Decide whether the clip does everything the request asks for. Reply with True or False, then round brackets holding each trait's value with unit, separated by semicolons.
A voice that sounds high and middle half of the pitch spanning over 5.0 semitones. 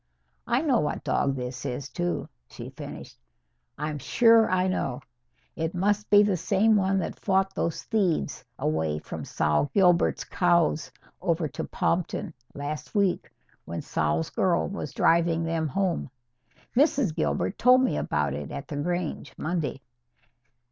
False (170 Hz; 5.4 semitones)